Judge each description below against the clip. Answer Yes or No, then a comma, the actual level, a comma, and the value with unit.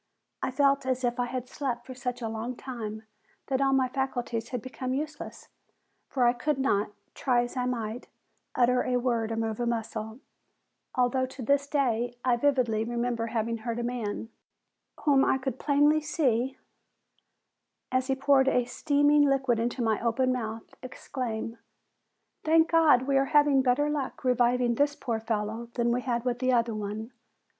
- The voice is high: Yes, very high, 250 Hz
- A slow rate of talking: No, average, 170 wpm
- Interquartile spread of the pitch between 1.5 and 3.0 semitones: Yes, narrow, 2.4 semitones